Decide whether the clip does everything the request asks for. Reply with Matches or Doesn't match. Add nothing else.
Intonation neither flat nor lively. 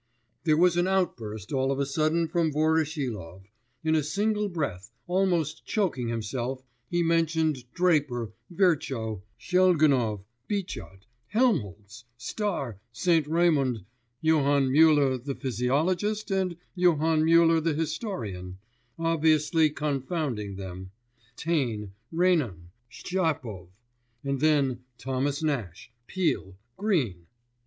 Doesn't match